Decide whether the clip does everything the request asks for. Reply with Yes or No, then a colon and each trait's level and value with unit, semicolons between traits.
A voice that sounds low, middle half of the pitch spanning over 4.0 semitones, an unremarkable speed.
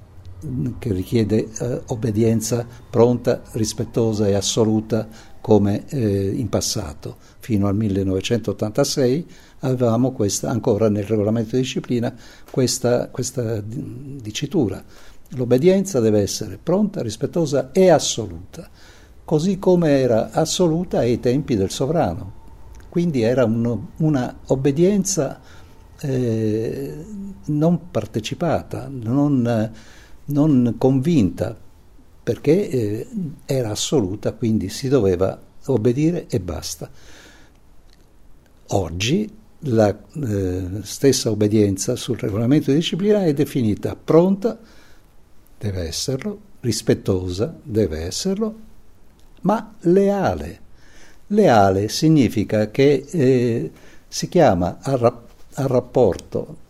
No: low, 120 Hz; average, 5.3 semitones; slow, 95 wpm